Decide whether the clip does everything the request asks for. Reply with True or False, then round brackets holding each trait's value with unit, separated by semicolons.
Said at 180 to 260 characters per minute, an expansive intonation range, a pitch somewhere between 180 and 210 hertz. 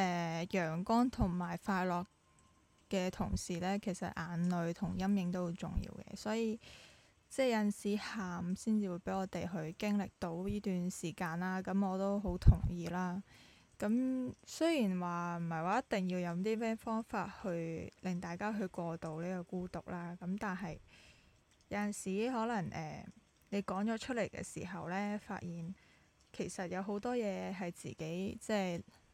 False (245 characters per minute; 2.8 semitones; 190 Hz)